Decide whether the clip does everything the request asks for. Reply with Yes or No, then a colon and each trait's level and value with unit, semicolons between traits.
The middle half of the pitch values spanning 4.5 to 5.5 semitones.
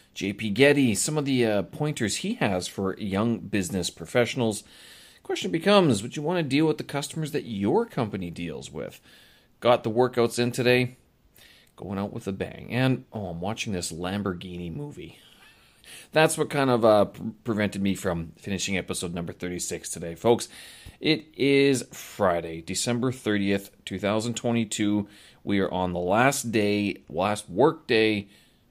Yes: average, 5.1 semitones